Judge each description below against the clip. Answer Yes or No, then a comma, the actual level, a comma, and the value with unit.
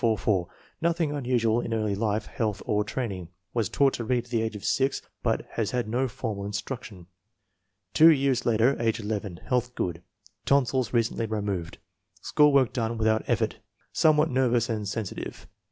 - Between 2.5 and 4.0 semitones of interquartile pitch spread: Yes, average, 3.3 semitones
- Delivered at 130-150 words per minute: No, average, 160 wpm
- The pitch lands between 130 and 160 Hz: No, low, 115 Hz